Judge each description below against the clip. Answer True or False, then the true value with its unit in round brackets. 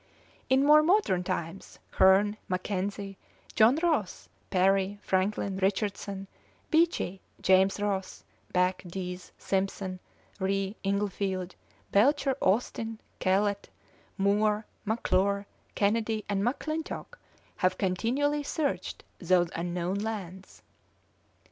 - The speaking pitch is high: True (200 Hz)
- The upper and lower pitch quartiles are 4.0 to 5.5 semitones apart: False (2.7 semitones)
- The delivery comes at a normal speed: False (90 wpm)